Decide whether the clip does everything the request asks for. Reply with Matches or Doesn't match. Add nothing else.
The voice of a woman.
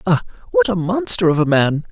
Doesn't match